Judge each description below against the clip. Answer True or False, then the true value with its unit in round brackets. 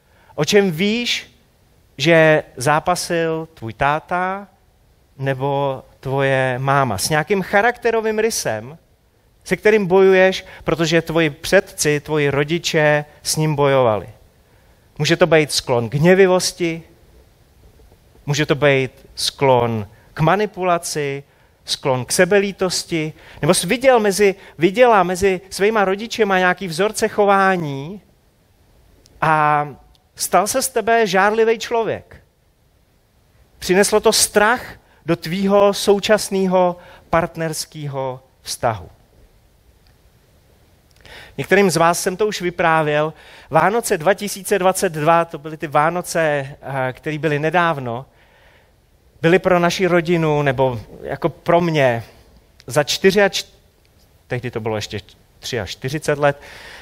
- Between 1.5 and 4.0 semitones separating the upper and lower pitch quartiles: False (5.8 semitones)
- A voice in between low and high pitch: True (160 Hz)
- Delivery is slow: True (105 wpm)